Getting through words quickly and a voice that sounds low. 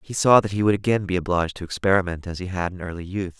Yes: fast, 285 wpm; very low, 95 Hz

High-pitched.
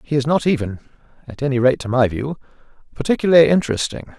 No: low, 135 Hz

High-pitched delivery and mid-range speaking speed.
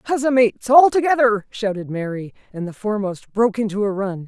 Yes: high, 220 Hz; average, 180 wpm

